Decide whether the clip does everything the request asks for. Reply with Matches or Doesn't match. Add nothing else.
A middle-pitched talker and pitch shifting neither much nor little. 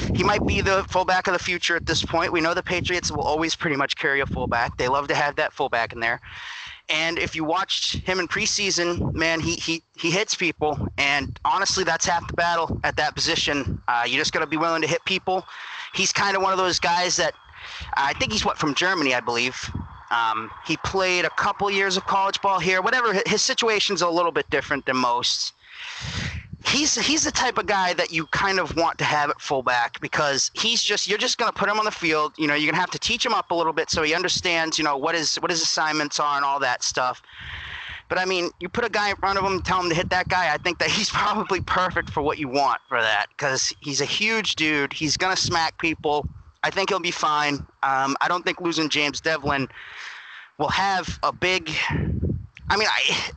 Matches